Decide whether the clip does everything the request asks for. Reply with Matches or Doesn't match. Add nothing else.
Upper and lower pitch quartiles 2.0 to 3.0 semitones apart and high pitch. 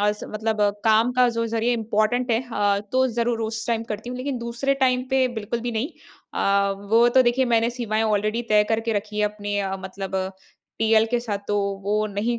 Matches